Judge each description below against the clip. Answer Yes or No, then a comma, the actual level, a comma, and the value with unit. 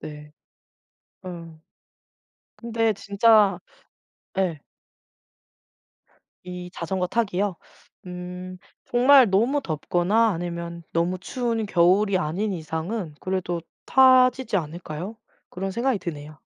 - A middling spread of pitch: Yes, average, 4.6 semitones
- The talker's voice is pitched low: No, medium, 185 Hz